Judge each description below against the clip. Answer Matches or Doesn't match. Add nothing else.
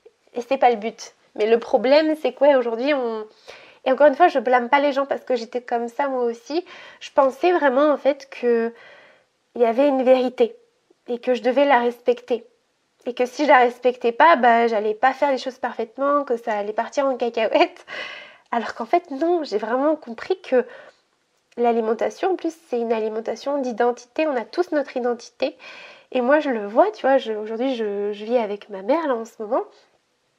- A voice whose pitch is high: Matches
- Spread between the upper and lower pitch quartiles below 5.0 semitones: Matches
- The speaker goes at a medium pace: Matches